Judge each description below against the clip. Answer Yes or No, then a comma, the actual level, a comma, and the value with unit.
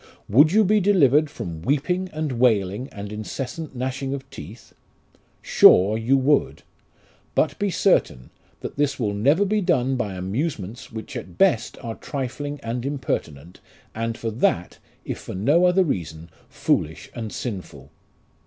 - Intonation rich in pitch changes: Yes, wide, 6.4 semitones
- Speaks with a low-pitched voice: Yes, low, 125 Hz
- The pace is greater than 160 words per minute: No, average, 145 wpm